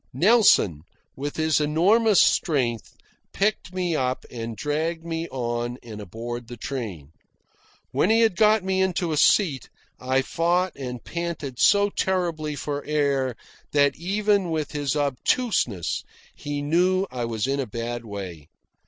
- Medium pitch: Yes, medium, 145 Hz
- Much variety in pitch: Yes, wide, 6.6 semitones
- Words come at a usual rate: Yes, average, 145 wpm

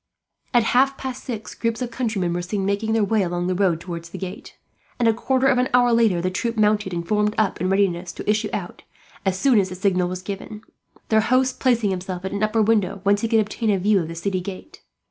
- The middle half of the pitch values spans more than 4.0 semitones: No, average, 3.6 semitones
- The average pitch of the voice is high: Yes, high, 205 Hz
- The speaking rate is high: Yes, fast, 240 wpm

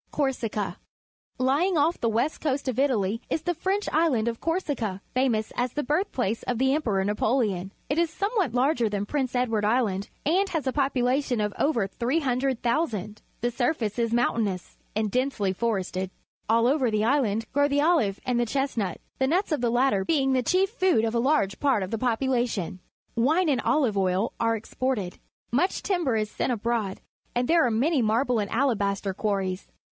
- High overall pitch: Yes, high, 245 Hz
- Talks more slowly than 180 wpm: No, average, 185 wpm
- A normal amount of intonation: Yes, average, 4.8 semitones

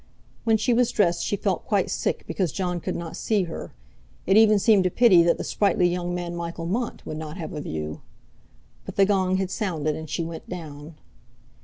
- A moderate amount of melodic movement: Yes, average, 3.3 semitones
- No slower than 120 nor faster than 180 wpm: No, fast, 205 wpm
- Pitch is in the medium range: Yes, medium, 180 Hz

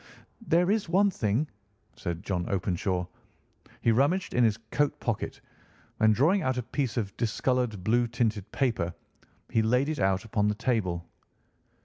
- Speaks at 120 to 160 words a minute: Yes, average, 150 wpm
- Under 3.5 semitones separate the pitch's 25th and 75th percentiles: No, average, 5.2 semitones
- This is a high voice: No, low, 115 Hz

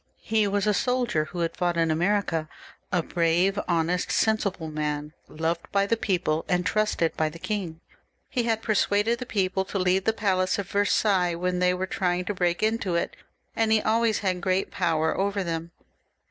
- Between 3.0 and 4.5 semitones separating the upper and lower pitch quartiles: Yes, average, 3.6 semitones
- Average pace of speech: Yes, average, 185 wpm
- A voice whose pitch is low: No, medium, 185 Hz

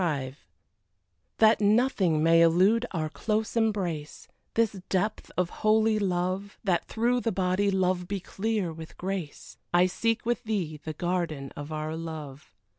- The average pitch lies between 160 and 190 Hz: Yes, medium, 185 Hz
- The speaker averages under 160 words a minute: Yes, average, 145 wpm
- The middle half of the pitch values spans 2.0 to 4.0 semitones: No, average, 4.7 semitones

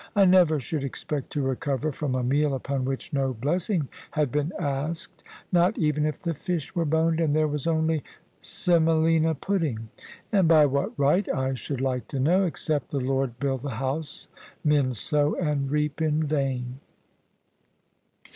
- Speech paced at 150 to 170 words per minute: Yes, average, 165 wpm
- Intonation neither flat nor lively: Yes, average, 3.1 semitones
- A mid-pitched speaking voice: Yes, medium, 150 Hz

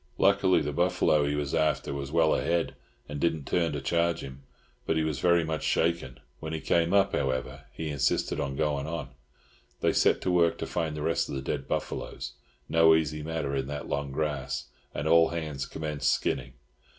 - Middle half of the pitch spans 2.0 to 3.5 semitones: Yes, average, 2.8 semitones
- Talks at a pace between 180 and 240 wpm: Yes, average, 190 wpm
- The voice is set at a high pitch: No, very low, 75 Hz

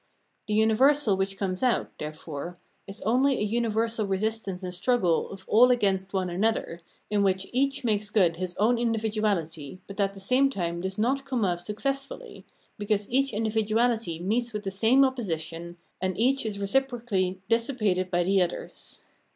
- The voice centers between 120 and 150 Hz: No, high, 210 Hz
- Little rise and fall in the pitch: No, average, 4.2 semitones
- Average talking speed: Yes, average, 165 wpm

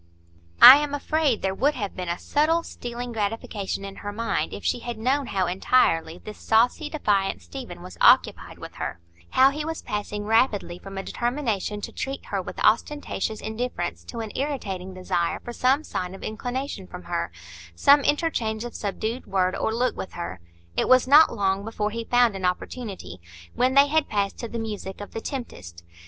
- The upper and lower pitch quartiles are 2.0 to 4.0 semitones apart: No, average, 5.0 semitones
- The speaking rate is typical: Yes, average, 185 wpm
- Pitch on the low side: No, high, 220 Hz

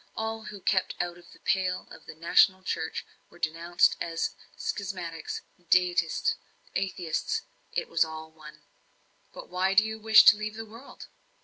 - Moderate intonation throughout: Yes, average, 4.2 semitones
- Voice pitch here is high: No, medium, 180 Hz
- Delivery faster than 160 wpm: No, average, 155 wpm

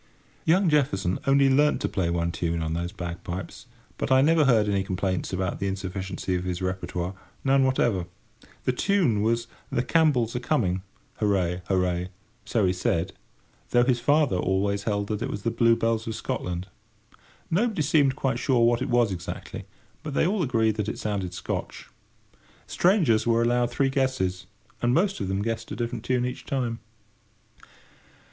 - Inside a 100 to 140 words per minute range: No, average, 165 wpm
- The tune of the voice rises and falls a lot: Yes, wide, 6.0 semitones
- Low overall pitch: Yes, low, 115 Hz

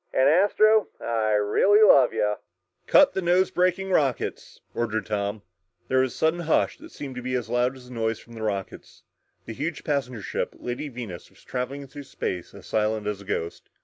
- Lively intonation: Yes, wide, 5.7 semitones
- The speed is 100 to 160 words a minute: No, average, 190 wpm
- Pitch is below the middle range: Yes, low, 125 Hz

